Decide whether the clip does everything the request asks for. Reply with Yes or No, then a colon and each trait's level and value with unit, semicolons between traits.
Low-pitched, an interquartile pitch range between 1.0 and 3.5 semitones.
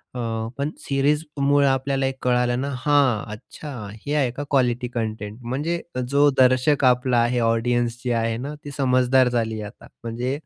Yes: low, 125 Hz; average, 2.8 semitones